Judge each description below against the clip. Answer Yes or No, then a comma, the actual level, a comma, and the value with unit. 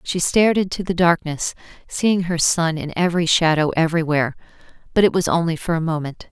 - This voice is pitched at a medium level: Yes, medium, 170 Hz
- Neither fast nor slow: Yes, average, 180 wpm